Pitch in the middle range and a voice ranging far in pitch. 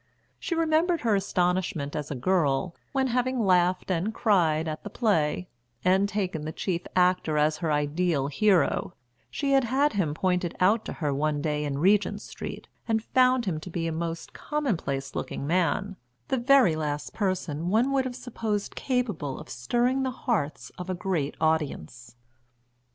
Yes: medium, 180 Hz; wide, 6.8 semitones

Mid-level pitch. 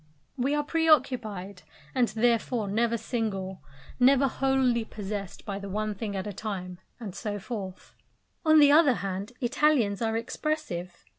No: high, 225 Hz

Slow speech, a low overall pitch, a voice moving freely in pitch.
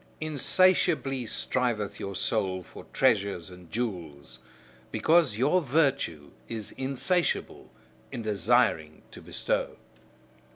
Yes: slow, 95 wpm; low, 115 Hz; wide, 6.8 semitones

